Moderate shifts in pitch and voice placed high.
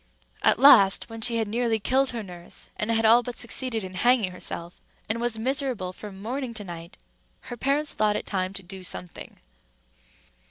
Yes: average, 4.2 semitones; high, 225 Hz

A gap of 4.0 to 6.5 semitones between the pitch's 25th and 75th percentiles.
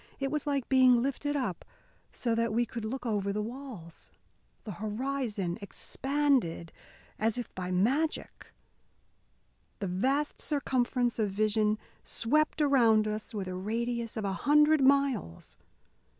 Yes: average, 4.6 semitones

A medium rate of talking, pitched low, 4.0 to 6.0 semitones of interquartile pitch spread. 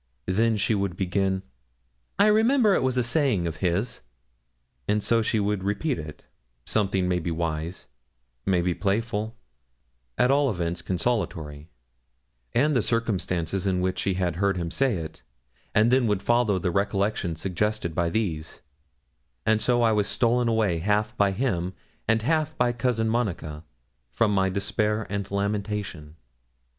Yes: average, 150 wpm; low, 100 Hz; average, 4.4 semitones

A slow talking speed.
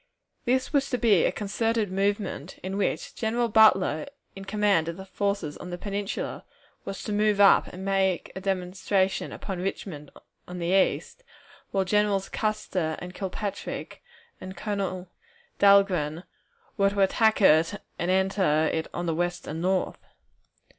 No: average, 145 wpm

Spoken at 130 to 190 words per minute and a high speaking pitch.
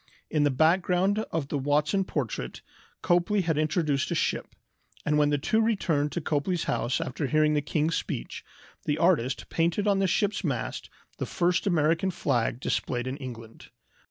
No: average, 165 wpm; medium, 155 Hz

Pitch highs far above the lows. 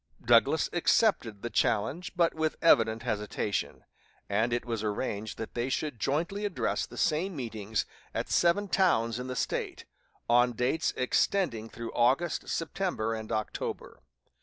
Yes: wide, 6.7 semitones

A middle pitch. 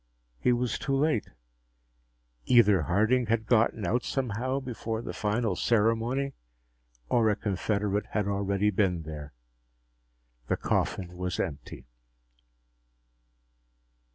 No: low, 110 Hz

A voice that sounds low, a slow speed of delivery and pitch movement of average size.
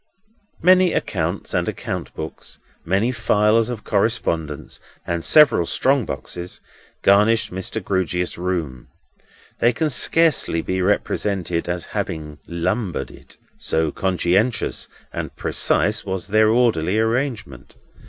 Yes: low, 100 Hz; slow, 115 wpm; average, 4.7 semitones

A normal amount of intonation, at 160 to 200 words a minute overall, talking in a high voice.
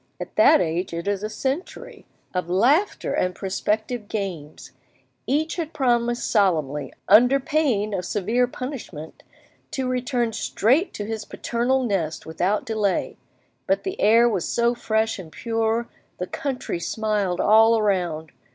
No: average, 4.6 semitones; average, 140 wpm; high, 220 Hz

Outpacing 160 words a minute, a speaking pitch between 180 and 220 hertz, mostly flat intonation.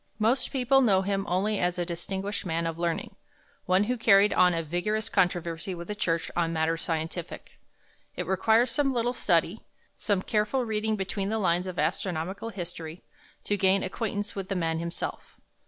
No: average, 170 wpm; high, 190 Hz; average, 3.7 semitones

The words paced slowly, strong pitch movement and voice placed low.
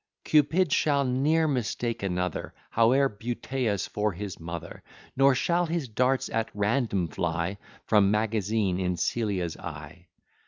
Yes: slow, 125 wpm; wide, 6.5 semitones; low, 110 Hz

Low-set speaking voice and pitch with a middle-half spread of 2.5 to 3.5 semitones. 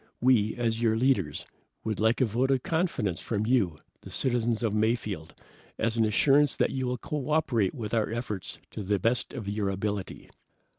Yes: low, 115 Hz; average, 3.2 semitones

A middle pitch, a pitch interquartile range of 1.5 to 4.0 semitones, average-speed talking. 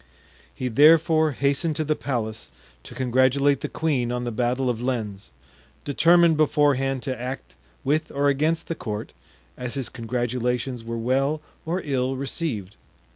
No: low, 130 Hz; average, 3.4 semitones; average, 145 wpm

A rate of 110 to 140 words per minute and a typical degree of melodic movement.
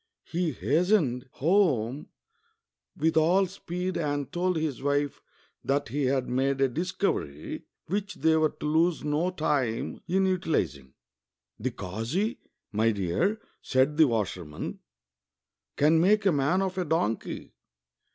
No: slow, 135 wpm; wide, 6.4 semitones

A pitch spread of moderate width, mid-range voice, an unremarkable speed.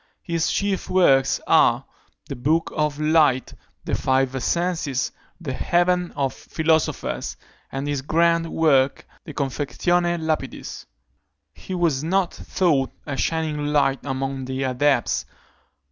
No: average, 3.8 semitones; medium, 150 Hz; slow, 120 wpm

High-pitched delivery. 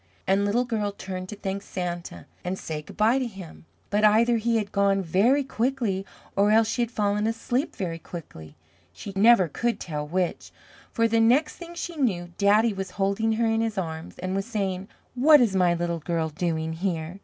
Yes: high, 200 Hz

